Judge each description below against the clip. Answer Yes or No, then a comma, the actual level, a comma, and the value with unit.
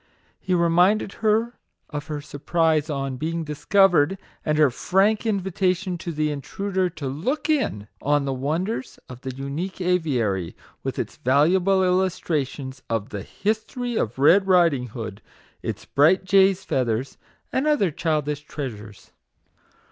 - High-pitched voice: No, medium, 160 Hz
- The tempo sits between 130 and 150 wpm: Yes, average, 145 wpm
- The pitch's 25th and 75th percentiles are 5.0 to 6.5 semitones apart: Yes, wide, 5.6 semitones